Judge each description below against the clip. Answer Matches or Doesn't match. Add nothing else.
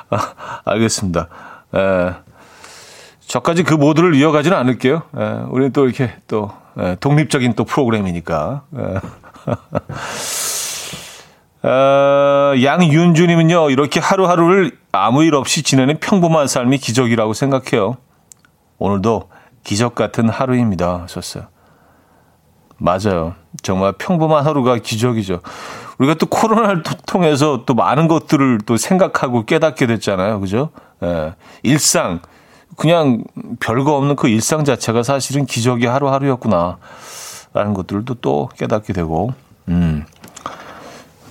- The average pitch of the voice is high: Doesn't match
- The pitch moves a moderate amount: Doesn't match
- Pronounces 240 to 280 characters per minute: Matches